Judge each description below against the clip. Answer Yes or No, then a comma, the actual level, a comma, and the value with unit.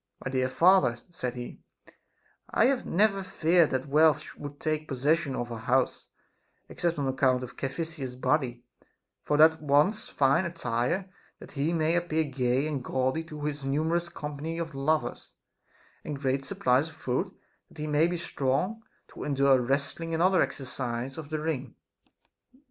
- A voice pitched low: No, medium, 145 Hz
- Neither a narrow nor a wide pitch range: Yes, average, 3.7 semitones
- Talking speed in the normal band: Yes, average, 160 wpm